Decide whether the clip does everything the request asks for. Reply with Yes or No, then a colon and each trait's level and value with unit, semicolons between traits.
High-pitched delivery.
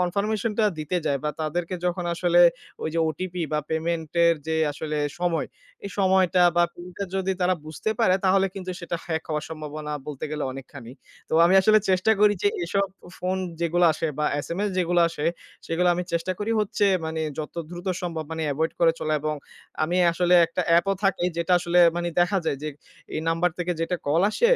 No: medium, 175 Hz